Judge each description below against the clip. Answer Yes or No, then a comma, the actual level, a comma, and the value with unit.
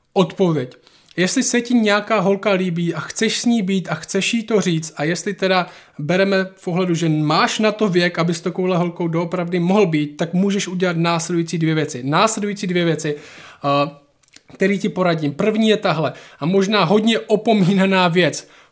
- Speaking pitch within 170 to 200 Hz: Yes, medium, 185 Hz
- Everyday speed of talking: No, fast, 175 wpm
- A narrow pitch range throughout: No, average, 3.5 semitones